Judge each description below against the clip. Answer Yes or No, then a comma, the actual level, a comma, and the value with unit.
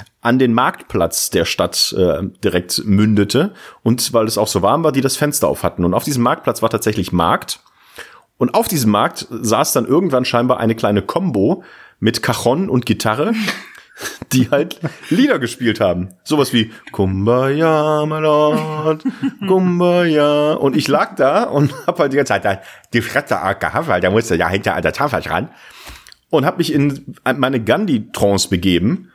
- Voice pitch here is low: Yes, low, 125 Hz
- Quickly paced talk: No, average, 165 wpm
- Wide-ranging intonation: Yes, wide, 5.7 semitones